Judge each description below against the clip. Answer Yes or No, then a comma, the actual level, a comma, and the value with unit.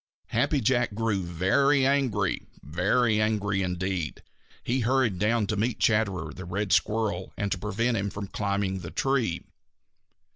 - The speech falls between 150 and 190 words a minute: No, average, 140 wpm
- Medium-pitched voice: No, low, 105 Hz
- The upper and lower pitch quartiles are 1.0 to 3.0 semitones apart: No, average, 3.7 semitones